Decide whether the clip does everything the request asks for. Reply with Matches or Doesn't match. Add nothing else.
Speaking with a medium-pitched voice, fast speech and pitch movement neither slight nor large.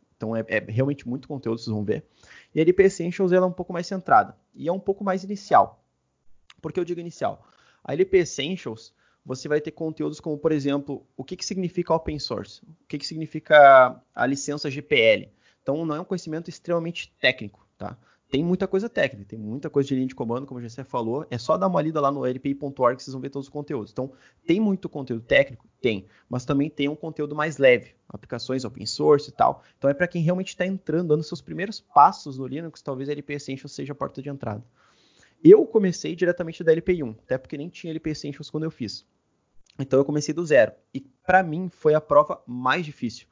Matches